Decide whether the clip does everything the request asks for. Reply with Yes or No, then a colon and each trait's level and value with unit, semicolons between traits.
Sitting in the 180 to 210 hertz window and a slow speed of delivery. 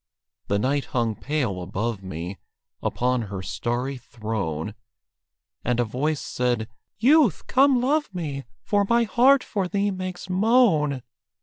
No: medium, 140 Hz; slow, 130 wpm